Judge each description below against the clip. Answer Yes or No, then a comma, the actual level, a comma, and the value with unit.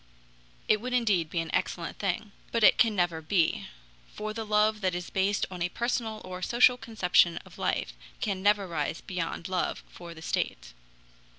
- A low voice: No, high, 190 Hz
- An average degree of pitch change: Yes, average, 3.7 semitones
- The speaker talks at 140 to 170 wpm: No, average, 180 wpm